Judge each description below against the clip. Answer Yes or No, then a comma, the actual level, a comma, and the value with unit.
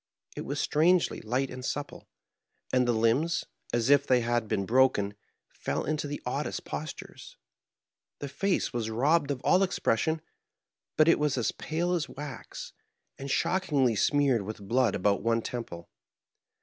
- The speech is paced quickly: No, average, 155 wpm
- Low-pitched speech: Yes, low, 130 Hz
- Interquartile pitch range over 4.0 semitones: Yes, average, 4.6 semitones